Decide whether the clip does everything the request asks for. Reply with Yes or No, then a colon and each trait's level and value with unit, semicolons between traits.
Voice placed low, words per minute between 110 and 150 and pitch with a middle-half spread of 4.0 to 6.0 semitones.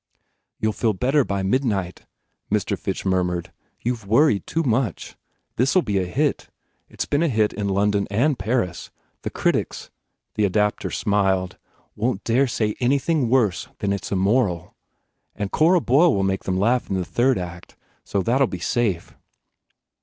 No: low, 105 Hz; average, 180 wpm; average, 4.8 semitones